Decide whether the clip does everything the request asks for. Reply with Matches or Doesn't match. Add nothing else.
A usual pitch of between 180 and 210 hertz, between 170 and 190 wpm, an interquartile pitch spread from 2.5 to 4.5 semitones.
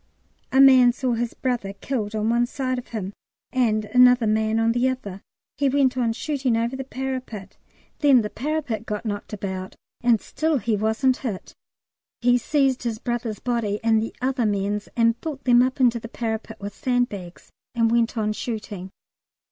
Doesn't match